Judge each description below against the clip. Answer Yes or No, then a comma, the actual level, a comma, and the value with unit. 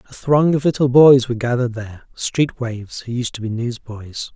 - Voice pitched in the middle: No, low, 125 Hz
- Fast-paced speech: No, average, 195 wpm